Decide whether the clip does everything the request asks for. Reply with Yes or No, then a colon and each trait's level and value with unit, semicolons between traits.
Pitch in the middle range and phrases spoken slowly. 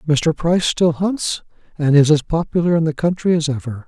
No: medium, 160 Hz; average, 200 wpm